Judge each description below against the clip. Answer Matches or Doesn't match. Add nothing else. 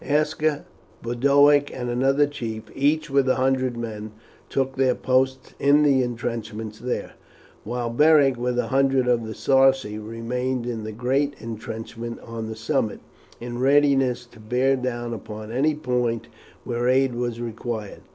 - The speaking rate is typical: Matches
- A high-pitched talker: Doesn't match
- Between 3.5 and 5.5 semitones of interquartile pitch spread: Doesn't match